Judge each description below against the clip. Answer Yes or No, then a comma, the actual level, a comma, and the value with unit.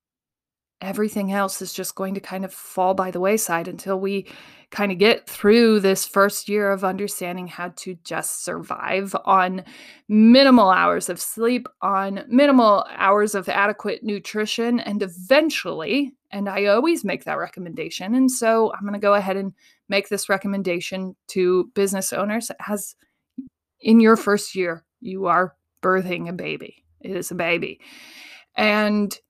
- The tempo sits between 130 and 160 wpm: Yes, average, 155 wpm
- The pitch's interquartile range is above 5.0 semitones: No, average, 2.9 semitones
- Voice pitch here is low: No, high, 200 Hz